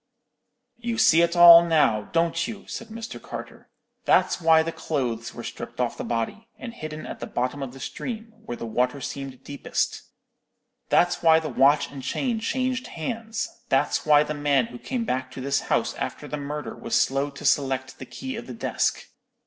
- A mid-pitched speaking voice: Yes, medium, 155 Hz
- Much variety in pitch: Yes, wide, 8.5 semitones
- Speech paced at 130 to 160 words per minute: No, average, 190 wpm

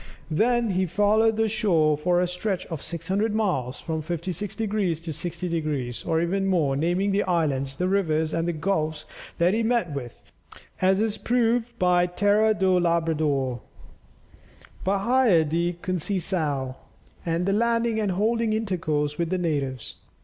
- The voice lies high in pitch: No, medium, 180 Hz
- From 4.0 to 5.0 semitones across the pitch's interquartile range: Yes, average, 4.6 semitones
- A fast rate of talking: No, average, 150 wpm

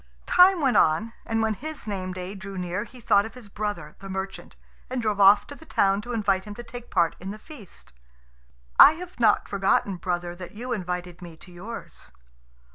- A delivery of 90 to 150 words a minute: No, average, 200 wpm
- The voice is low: No, high, 205 Hz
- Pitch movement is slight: No, average, 4.1 semitones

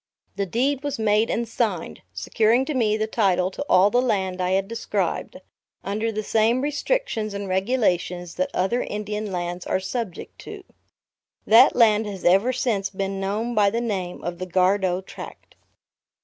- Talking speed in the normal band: Yes, average, 165 wpm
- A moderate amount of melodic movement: Yes, average, 3.7 semitones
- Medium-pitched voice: No, high, 210 Hz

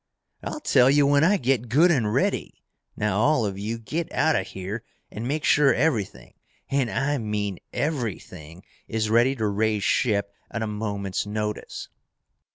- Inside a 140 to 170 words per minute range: Yes, average, 165 wpm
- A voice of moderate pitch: No, low, 110 Hz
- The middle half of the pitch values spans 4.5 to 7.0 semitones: Yes, average, 5.0 semitones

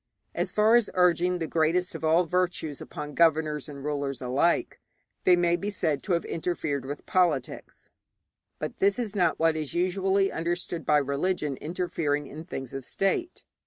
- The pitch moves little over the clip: No, average, 3.4 semitones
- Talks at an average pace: Yes, average, 165 wpm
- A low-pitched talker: No, medium, 165 Hz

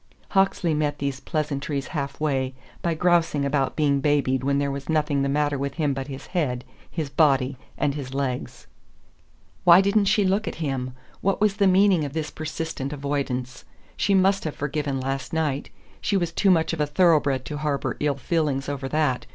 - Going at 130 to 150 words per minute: No, average, 185 wpm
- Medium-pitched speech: Yes, medium, 145 Hz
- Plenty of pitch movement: No, average, 3.0 semitones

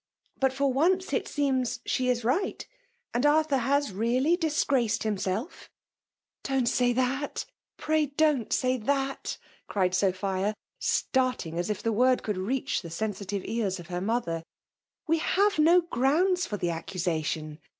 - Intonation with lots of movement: Yes, wide, 6.2 semitones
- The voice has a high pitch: Yes, very high, 250 Hz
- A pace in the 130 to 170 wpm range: Yes, average, 155 wpm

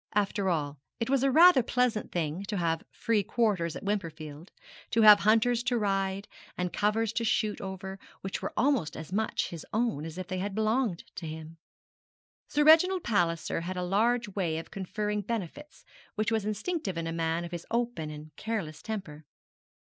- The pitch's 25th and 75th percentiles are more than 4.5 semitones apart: Yes, average, 5.2 semitones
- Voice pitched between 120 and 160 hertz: No, high, 200 Hz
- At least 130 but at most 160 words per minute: No, average, 180 wpm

